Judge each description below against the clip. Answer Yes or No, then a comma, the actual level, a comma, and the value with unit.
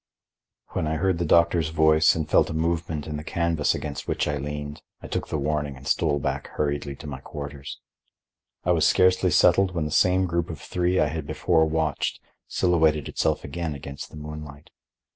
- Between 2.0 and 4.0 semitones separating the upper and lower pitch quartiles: Yes, narrow, 2.5 semitones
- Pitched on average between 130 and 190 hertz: No, very low, 75 Hz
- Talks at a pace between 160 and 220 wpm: Yes, average, 190 wpm